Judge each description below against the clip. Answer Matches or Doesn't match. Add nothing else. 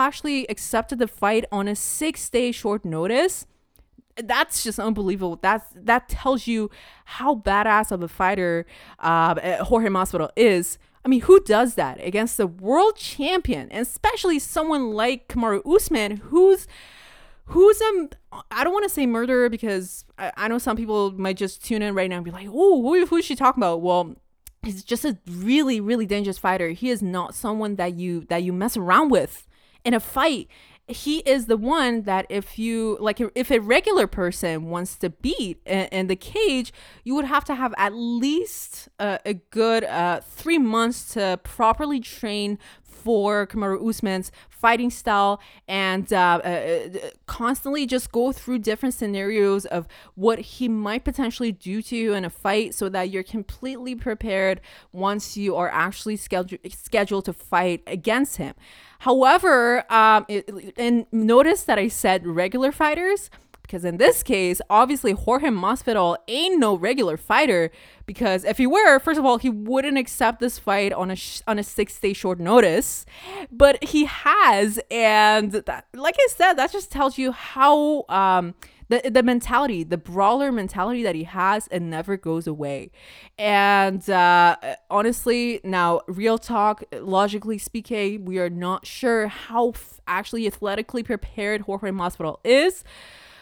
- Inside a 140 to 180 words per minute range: Matches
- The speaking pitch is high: Matches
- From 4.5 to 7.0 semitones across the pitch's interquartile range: Matches